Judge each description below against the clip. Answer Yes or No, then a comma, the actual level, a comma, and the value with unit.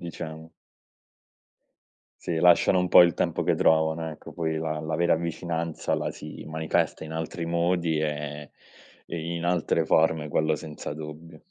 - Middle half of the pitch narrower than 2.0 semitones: Yes, narrow, 1.4 semitones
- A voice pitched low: Yes, very low, 80 Hz